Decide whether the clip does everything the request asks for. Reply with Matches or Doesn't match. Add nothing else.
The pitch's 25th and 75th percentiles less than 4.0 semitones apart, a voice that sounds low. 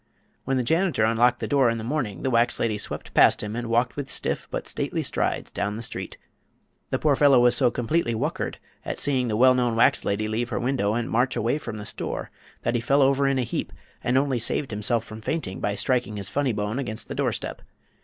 Matches